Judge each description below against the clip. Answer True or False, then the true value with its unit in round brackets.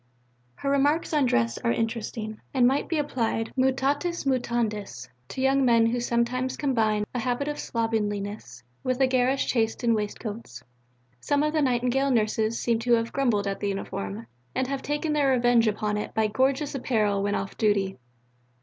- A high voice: True (235 Hz)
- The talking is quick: False (175 wpm)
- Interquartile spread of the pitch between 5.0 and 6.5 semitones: False (3.9 semitones)